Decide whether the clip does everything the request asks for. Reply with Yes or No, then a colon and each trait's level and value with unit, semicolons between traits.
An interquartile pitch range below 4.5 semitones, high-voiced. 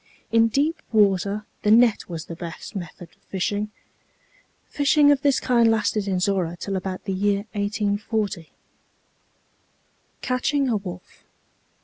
Yes: average, 3.3 semitones; high, 205 Hz